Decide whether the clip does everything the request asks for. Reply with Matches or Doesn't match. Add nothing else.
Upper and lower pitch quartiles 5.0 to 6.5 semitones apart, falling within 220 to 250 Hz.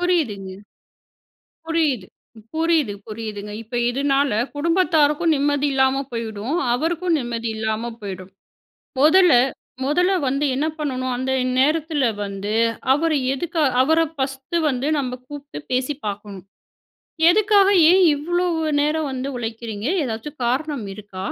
Doesn't match